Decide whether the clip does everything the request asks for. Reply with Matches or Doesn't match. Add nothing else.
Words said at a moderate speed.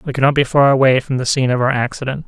Doesn't match